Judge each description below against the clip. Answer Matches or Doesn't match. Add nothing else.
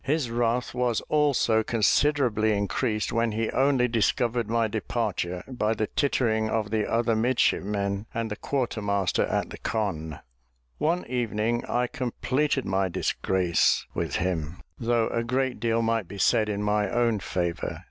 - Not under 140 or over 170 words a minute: Matches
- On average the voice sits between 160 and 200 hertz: Doesn't match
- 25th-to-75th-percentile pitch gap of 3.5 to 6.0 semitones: Doesn't match